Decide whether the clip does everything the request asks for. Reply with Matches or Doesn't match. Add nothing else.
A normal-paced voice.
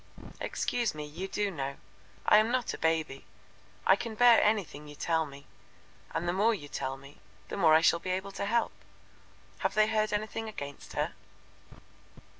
Matches